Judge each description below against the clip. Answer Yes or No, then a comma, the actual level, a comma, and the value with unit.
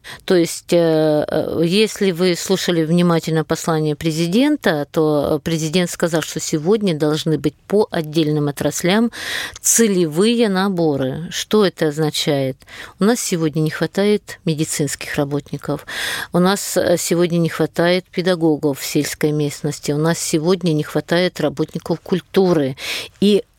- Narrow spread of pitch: No, average, 3.2 semitones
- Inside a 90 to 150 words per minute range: Yes, average, 120 wpm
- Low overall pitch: No, medium, 165 Hz